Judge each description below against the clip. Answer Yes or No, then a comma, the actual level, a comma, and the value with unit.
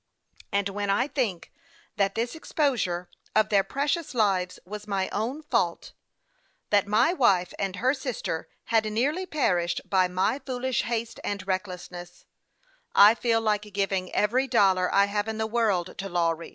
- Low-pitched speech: No, high, 210 Hz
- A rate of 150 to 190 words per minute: Yes, average, 155 wpm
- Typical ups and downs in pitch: Yes, average, 4.1 semitones